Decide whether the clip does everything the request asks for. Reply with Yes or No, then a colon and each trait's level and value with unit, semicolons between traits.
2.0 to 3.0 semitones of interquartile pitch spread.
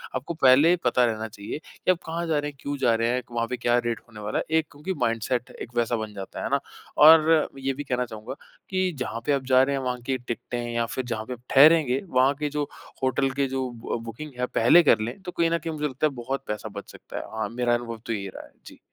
No: average, 3.8 semitones